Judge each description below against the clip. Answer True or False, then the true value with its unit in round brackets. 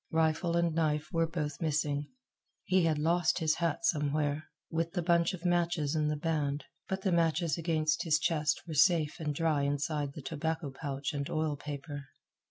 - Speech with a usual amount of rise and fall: False (2.1 semitones)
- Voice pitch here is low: False (155 Hz)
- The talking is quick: False (180 wpm)